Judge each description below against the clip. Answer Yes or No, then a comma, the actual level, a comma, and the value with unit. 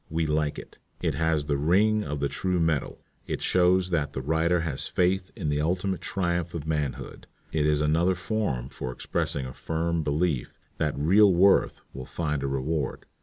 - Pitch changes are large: No, average, 3.3 semitones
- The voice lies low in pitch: Yes, very low, 80 Hz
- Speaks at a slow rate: No, average, 180 wpm